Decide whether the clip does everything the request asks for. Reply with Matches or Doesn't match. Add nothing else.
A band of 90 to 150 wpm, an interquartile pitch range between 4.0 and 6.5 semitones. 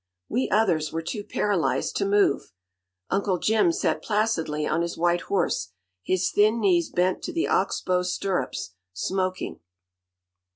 Doesn't match